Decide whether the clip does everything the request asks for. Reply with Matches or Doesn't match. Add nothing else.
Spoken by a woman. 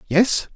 Doesn't match